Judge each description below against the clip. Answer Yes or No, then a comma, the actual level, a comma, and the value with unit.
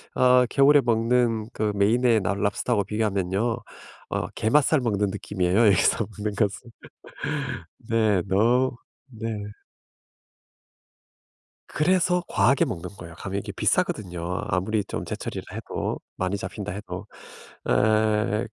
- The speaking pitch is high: No, low, 110 Hz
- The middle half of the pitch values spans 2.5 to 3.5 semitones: Yes, average, 3.1 semitones